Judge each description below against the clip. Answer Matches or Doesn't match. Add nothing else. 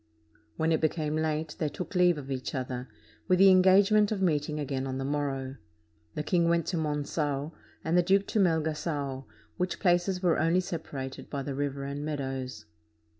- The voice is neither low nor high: Matches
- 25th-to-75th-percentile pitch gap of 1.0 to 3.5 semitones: Doesn't match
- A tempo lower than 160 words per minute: Doesn't match